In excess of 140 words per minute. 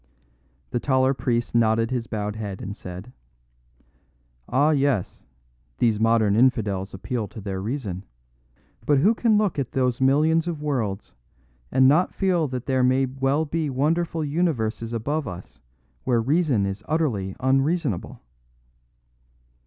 No: slow, 135 wpm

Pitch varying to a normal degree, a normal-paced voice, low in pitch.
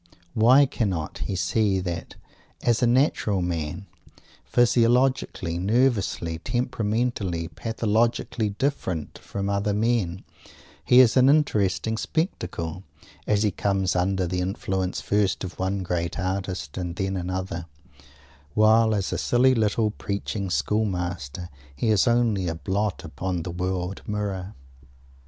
No: average, 3.8 semitones; slow, 125 wpm; low, 100 Hz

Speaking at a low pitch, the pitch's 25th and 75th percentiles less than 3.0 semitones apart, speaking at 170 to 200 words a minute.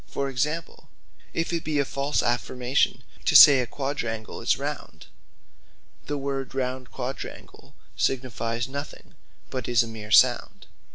No: low, 130 Hz; narrow, 2.6 semitones; slow, 135 wpm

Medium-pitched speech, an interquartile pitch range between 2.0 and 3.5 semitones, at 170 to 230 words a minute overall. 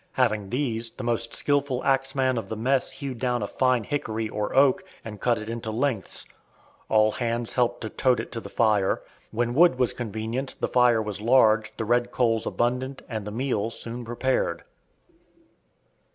No: low, 120 Hz; average, 2.8 semitones; average, 175 wpm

